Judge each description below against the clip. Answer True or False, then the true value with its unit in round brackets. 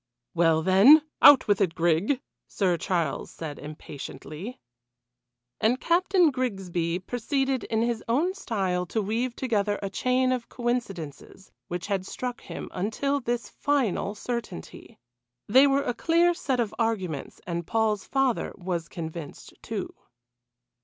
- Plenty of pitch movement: True (6.3 semitones)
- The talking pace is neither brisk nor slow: False (130 wpm)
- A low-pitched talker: False (220 Hz)